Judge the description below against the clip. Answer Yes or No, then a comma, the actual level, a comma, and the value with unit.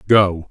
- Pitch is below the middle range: Yes, very low, 95 Hz